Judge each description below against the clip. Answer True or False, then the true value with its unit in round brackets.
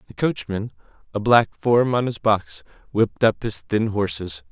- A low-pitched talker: True (110 Hz)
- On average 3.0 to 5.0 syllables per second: True (4.5 syllables/s)